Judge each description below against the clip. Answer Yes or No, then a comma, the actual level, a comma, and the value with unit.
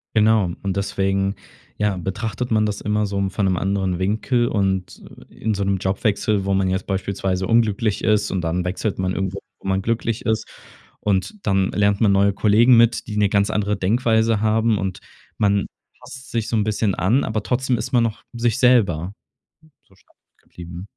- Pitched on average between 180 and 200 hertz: No, low, 100 Hz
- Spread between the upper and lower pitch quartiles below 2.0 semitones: No, narrow, 2.5 semitones